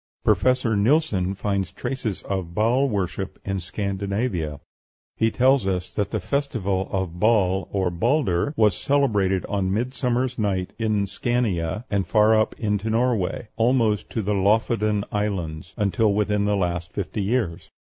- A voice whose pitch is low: Yes, low, 105 Hz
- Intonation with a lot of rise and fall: No, average, 3.4 semitones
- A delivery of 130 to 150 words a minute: Yes, average, 140 wpm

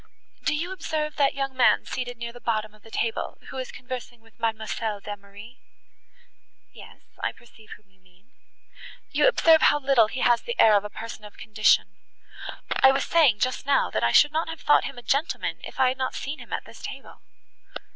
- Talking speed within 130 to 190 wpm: No, fast, 205 wpm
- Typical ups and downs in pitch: Yes, average, 4.3 semitones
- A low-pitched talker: No, high, 245 Hz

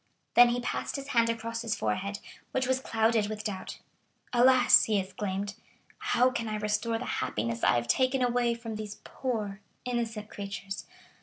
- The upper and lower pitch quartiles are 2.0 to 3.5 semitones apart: Yes, average, 3.1 semitones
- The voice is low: No, high, 225 Hz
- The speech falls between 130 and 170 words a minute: Yes, average, 165 wpm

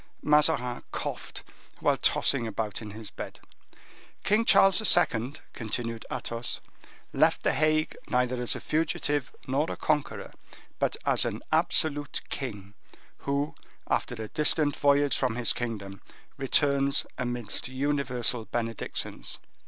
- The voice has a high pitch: No, low, 130 Hz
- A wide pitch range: No, average, 4.0 semitones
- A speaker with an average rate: No, slow, 120 wpm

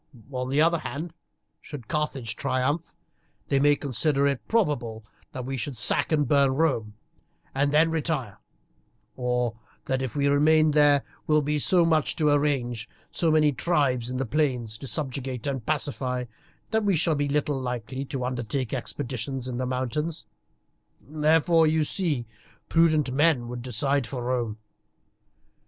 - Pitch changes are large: No, average, 3.4 semitones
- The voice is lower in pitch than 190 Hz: Yes, medium, 140 Hz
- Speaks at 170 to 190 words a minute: No, average, 150 wpm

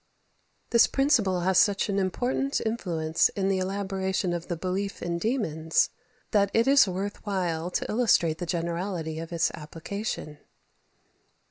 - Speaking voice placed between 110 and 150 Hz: No, high, 190 Hz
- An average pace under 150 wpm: Yes, average, 140 wpm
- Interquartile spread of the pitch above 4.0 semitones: No, average, 3.3 semitones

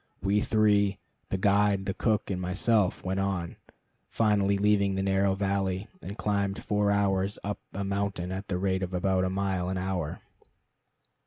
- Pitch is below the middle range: Yes, low, 100 Hz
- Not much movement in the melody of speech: Yes, narrow, 1.3 semitones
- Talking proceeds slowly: No, average, 165 wpm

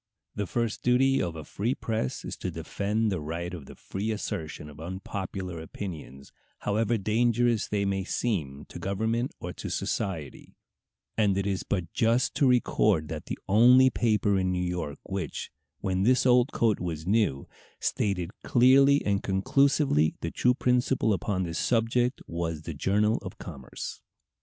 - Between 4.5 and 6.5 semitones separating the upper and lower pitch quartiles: Yes, average, 5.2 semitones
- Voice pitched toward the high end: No, low, 100 Hz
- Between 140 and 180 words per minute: Yes, average, 160 wpm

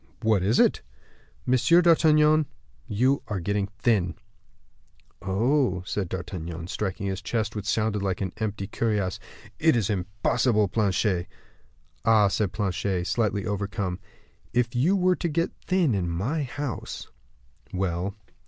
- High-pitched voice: No, low, 105 Hz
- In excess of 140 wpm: No, slow, 135 wpm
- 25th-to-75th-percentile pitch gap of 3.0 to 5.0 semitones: Yes, average, 4.4 semitones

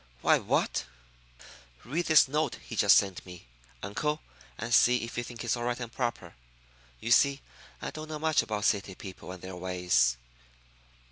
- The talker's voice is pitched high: No, low, 115 Hz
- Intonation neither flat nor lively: No, wide, 6.0 semitones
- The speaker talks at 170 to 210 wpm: Yes, average, 180 wpm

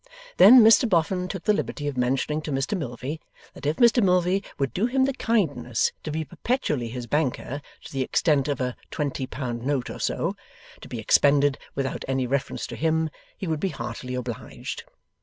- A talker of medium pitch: Yes, medium, 145 Hz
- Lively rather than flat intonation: Yes, wide, 5.8 semitones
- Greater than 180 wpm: Yes, average, 190 wpm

